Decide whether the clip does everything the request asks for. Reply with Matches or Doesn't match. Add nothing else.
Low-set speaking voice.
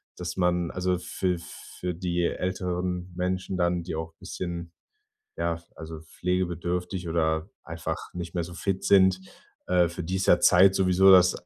Matches